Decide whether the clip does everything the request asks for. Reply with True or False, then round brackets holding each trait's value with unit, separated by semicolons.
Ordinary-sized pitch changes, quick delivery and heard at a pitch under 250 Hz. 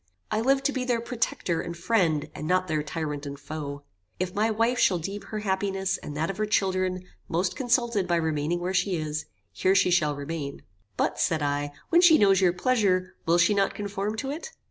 True (5.0 semitones; 210 wpm; 185 Hz)